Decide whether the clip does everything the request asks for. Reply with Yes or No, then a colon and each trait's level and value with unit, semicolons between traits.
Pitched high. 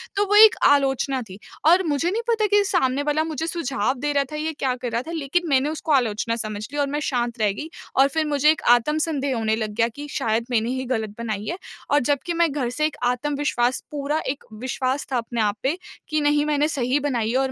Yes: very high, 280 Hz